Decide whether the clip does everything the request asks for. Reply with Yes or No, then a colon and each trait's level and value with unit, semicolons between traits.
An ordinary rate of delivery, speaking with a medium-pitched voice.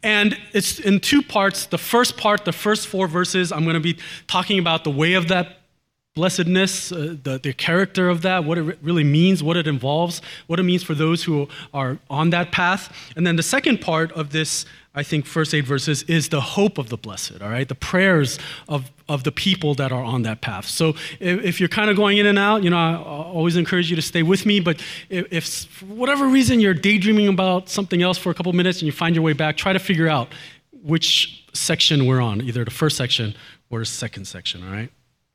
No: fast, 235 wpm; medium, 165 Hz